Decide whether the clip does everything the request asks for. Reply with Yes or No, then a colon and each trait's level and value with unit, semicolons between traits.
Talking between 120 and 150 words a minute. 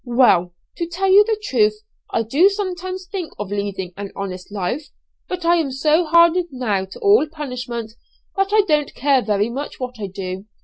No: average, 185 wpm